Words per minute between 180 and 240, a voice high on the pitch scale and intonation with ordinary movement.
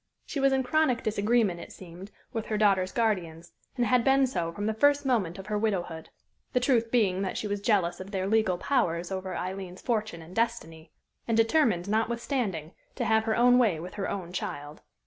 Yes: average, 200 wpm; high, 210 Hz; average, 4.5 semitones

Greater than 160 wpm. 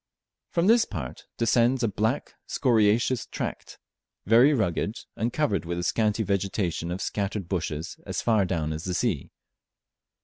No: average, 145 wpm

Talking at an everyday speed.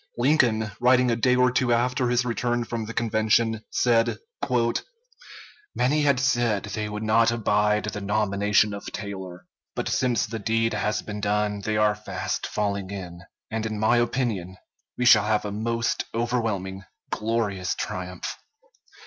Yes: average, 150 wpm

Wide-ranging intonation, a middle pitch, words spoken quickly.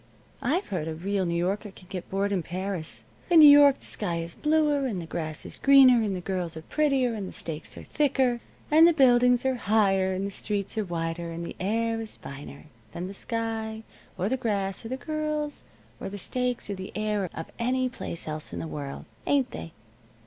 No: wide, 6.2 semitones; high, 205 Hz; fast, 215 wpm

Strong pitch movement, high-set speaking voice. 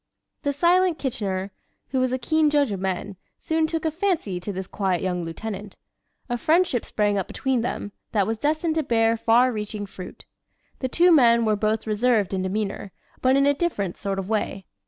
Yes: wide, 6.2 semitones; high, 225 Hz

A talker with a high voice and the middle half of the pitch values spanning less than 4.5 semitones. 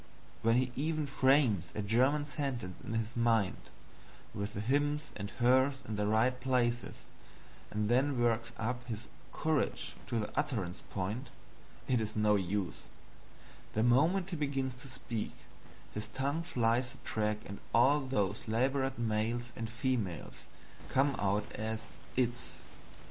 No: low, 120 Hz; average, 3.6 semitones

